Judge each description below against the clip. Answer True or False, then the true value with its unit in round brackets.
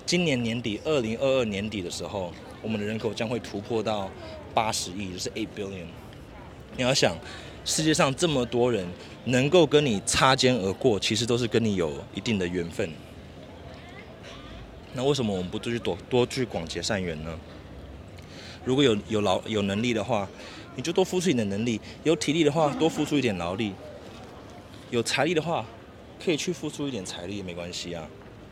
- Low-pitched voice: True (110 Hz)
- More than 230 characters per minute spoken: True (280 characters per minute)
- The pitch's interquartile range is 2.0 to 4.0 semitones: False (5.2 semitones)